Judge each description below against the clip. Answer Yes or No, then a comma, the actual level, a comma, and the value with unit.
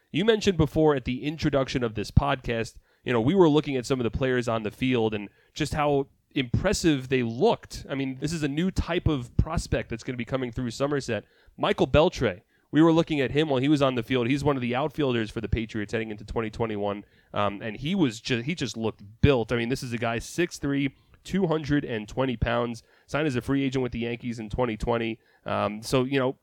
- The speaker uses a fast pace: Yes, fast, 225 wpm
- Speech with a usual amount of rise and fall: Yes, average, 4.0 semitones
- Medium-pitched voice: No, low, 125 Hz